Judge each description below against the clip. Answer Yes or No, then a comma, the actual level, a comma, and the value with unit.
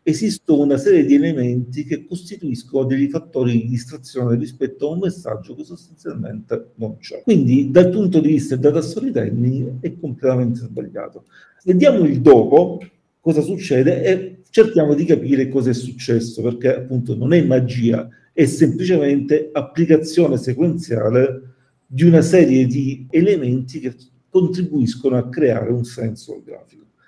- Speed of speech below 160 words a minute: Yes, average, 135 wpm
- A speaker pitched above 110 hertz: Yes, medium, 140 Hz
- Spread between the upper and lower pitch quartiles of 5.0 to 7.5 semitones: No, average, 4.5 semitones